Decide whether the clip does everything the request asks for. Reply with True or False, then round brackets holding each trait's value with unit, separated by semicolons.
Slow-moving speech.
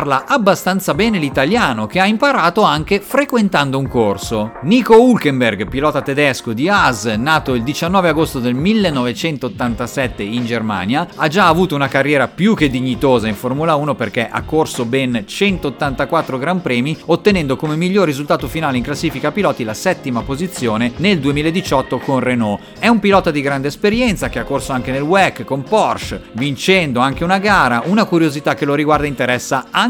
False (165 wpm)